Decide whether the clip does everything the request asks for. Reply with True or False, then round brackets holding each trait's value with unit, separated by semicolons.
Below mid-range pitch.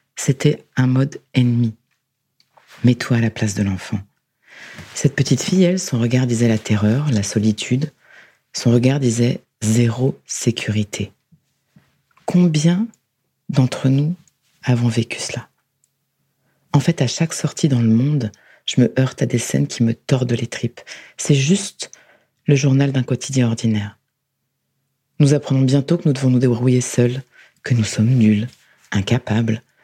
True (130 Hz)